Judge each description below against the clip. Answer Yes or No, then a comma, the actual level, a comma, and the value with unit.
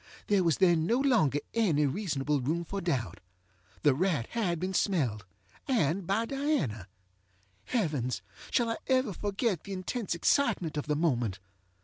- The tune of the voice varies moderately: No, wide, 6.7 semitones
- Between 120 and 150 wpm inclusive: Yes, average, 140 wpm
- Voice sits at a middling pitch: Yes, medium, 170 Hz